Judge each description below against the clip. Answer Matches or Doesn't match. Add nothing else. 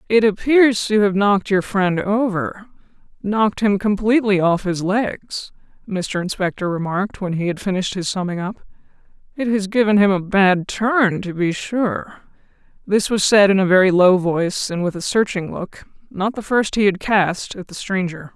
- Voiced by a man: Doesn't match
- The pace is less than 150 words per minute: Doesn't match